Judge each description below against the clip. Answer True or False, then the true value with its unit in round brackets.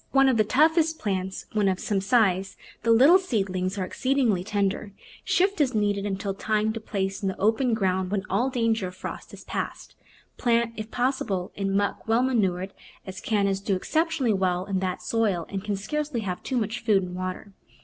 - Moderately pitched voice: False (205 Hz)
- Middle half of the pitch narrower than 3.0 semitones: False (3.8 semitones)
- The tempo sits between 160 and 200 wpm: True (195 wpm)